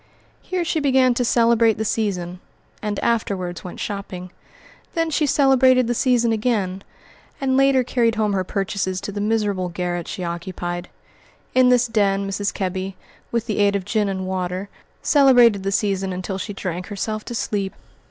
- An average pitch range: Yes, average, 4.0 semitones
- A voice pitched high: Yes, high, 205 Hz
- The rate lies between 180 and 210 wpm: No, average, 165 wpm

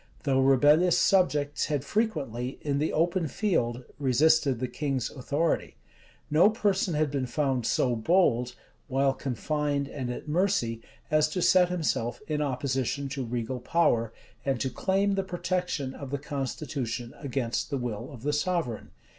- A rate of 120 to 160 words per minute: Yes, average, 150 wpm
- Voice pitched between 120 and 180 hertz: Yes, medium, 140 Hz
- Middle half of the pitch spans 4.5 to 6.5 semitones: No, average, 4.1 semitones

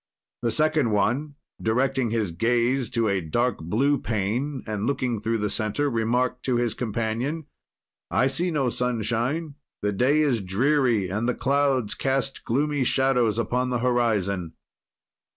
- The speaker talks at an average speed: Yes, average, 145 wpm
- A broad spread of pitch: No, average, 3.5 semitones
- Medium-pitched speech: No, low, 120 Hz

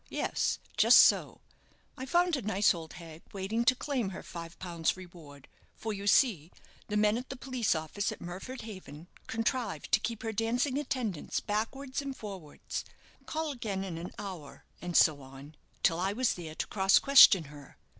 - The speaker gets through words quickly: No, average, 175 wpm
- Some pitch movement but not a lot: No, wide, 6.6 semitones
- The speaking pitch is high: Yes, high, 200 Hz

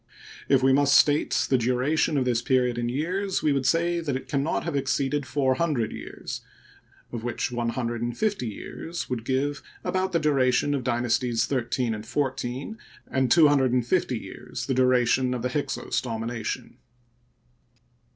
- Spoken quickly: No, average, 175 wpm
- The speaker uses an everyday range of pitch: Yes, average, 3.1 semitones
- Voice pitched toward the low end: Yes, low, 130 Hz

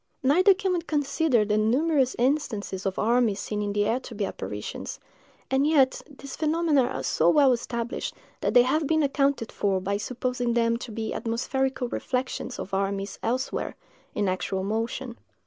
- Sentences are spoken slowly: No, average, 165 wpm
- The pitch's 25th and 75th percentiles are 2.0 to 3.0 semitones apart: No, average, 4.7 semitones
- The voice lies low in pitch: No, high, 245 Hz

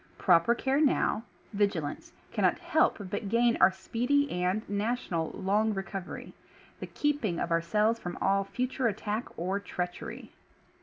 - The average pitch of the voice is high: Yes, high, 205 Hz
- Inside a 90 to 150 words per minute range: Yes, average, 145 wpm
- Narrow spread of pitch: No, average, 4.3 semitones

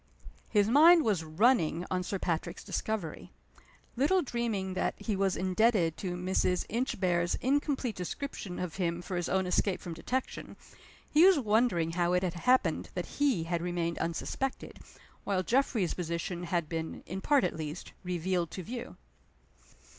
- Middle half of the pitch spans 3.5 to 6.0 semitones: Yes, wide, 5.4 semitones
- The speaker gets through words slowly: No, average, 155 wpm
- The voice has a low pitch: No, medium, 185 Hz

